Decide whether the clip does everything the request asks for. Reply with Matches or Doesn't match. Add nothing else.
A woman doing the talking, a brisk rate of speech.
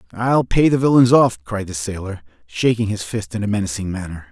Doesn't match